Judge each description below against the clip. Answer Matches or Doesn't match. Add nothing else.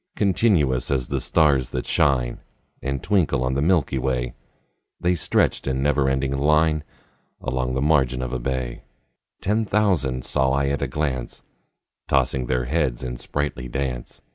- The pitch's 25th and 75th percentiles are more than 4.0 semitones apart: Doesn't match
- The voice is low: Matches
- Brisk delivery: Doesn't match